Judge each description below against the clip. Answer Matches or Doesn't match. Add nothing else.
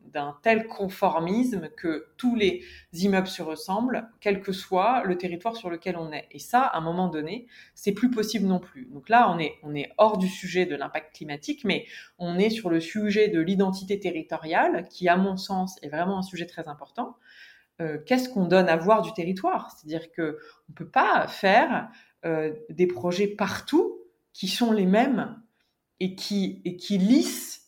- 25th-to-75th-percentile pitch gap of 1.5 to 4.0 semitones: Doesn't match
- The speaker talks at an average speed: Matches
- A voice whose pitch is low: Doesn't match